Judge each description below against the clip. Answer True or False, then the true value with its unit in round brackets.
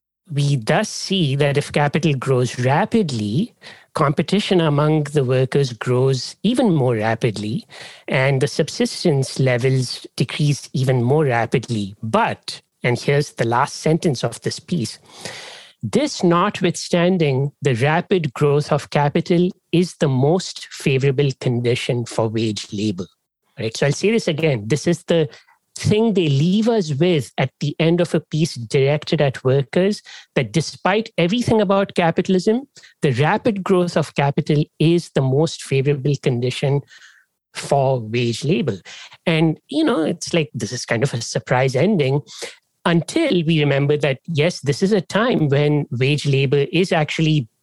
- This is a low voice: False (150 Hz)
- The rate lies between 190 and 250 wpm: False (145 wpm)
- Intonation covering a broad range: False (4.5 semitones)